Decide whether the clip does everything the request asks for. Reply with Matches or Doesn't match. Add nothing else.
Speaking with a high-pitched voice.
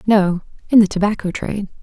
Matches